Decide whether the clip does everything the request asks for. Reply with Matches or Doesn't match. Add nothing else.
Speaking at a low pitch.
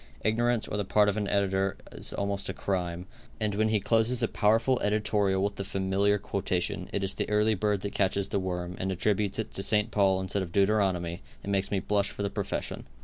Matches